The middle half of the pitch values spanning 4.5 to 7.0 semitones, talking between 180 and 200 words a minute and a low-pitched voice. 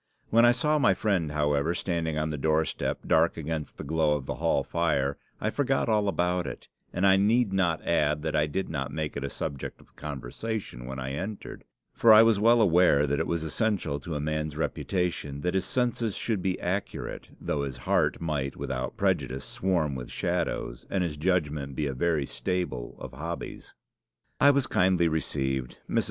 Yes: average, 4.8 semitones; average, 190 wpm; very low, 80 Hz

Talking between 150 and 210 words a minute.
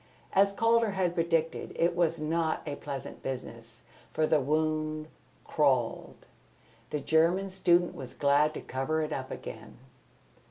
No: slow, 135 wpm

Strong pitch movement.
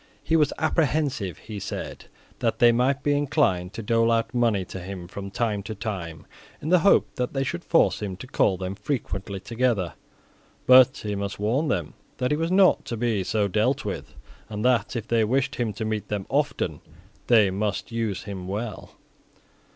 No: average, 4.6 semitones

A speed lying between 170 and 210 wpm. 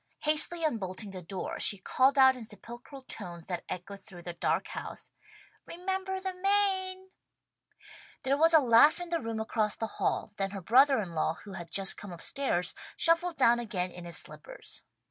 Yes: average, 185 wpm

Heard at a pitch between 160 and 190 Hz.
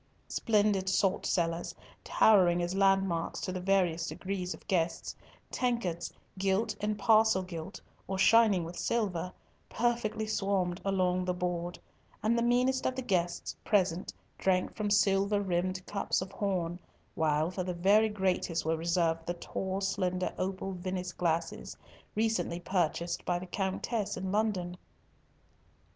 Yes: medium, 185 Hz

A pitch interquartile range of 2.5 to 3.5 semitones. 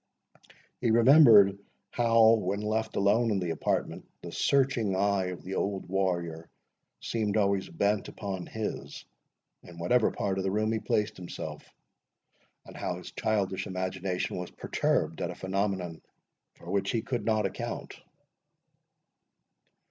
Yes: average, 2.8 semitones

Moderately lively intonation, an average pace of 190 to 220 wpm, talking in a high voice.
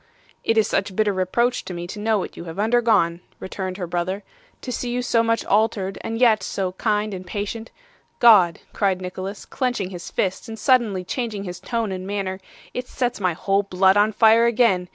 Yes: average, 3.4 semitones; average, 195 wpm; high, 205 Hz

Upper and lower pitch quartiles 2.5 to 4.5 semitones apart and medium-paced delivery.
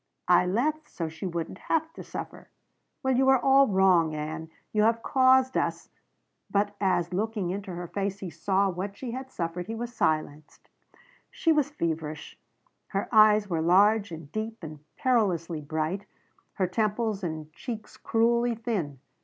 No: wide, 5.4 semitones; average, 160 wpm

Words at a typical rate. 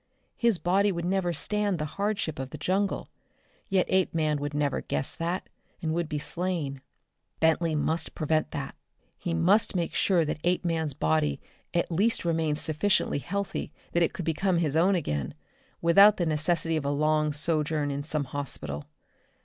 Yes: average, 165 wpm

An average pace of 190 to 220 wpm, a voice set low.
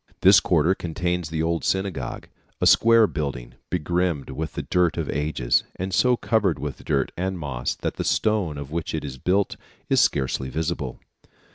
No: average, 170 wpm; very low, 80 Hz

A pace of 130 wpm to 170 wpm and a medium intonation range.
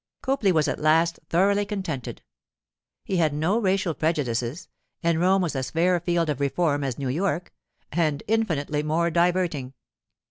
Yes: average, 150 wpm; average, 4.0 semitones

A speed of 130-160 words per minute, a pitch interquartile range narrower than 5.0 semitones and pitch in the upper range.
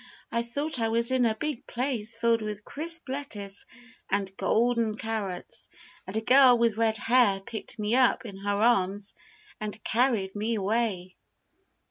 Yes: average, 155 wpm; average, 2.9 semitones; high, 225 Hz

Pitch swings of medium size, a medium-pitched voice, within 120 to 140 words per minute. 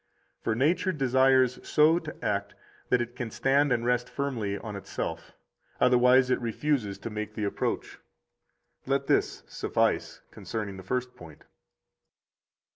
No: average, 3.7 semitones; low, 125 Hz; slow, 135 wpm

